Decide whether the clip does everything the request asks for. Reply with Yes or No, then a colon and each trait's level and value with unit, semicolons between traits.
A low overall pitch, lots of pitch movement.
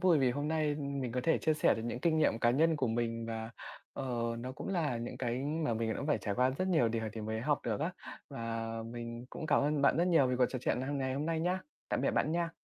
No: low, 130 Hz; average, 4.8 semitones